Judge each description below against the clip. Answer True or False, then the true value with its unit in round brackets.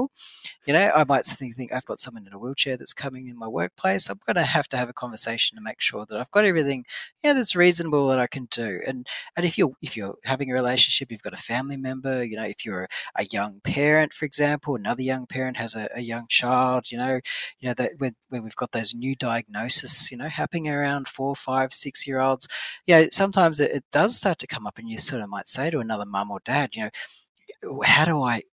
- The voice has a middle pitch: False (130 Hz)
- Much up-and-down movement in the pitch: False (3.2 semitones)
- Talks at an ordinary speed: False (250 wpm)